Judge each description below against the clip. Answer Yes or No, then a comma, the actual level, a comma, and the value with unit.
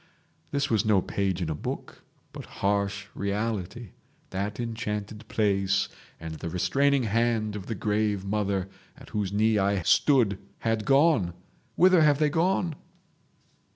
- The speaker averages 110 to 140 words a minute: Yes, slow, 135 wpm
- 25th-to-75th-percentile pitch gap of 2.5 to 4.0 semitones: Yes, average, 3.3 semitones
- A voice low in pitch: Yes, low, 105 Hz